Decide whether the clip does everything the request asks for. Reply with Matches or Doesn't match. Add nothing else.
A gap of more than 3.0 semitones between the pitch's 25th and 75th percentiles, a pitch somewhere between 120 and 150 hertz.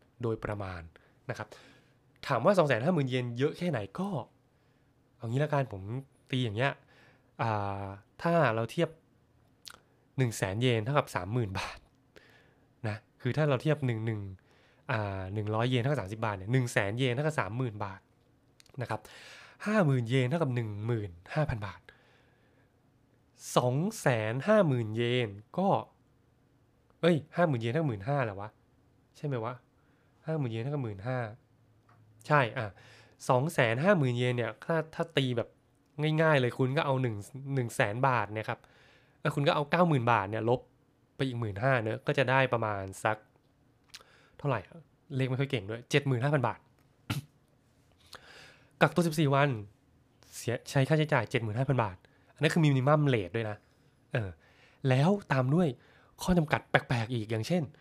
Matches